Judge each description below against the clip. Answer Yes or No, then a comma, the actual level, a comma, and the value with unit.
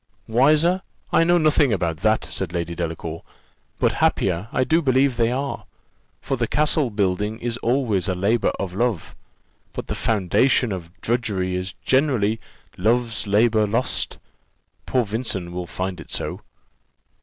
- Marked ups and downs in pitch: Yes, wide, 5.7 semitones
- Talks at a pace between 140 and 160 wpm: Yes, average, 145 wpm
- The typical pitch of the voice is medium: No, low, 110 Hz